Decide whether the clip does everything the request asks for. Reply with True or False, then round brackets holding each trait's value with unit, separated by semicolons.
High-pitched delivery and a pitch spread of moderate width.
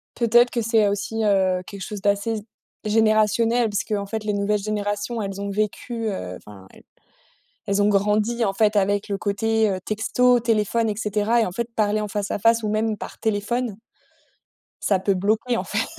False (210 Hz; 1.8 semitones)